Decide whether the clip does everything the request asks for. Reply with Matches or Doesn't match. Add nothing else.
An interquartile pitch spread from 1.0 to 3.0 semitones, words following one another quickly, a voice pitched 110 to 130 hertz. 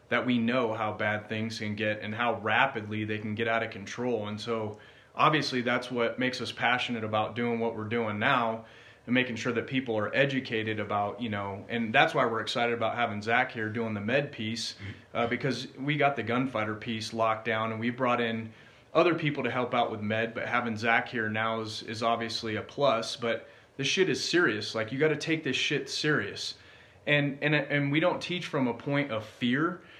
Matches